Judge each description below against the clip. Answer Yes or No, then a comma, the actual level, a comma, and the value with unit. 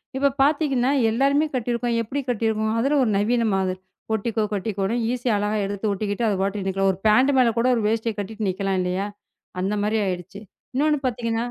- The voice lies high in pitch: Yes, high, 220 Hz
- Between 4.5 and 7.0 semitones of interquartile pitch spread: No, average, 3.6 semitones